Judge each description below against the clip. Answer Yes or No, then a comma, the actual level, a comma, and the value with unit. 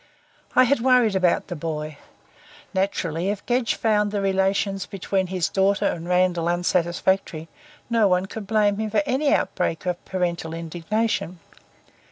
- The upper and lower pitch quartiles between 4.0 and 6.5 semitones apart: No, average, 3.3 semitones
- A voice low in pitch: No, high, 190 Hz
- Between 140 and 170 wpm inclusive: Yes, average, 145 wpm